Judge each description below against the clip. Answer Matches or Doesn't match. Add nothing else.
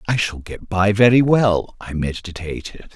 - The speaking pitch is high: Doesn't match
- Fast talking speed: Doesn't match